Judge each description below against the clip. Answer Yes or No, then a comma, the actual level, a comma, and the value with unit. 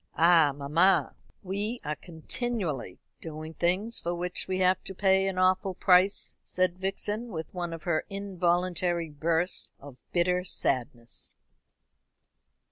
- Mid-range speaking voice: Yes, medium, 180 Hz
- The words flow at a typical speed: No, slow, 125 wpm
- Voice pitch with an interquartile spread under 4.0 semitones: Yes, average, 2.8 semitones